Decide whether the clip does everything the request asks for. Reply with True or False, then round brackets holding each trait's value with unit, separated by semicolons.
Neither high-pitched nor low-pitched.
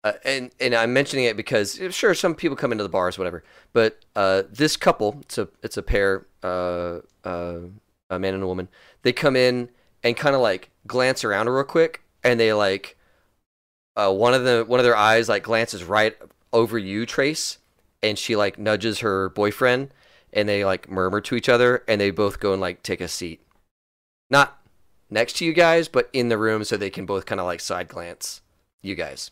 False (110 Hz)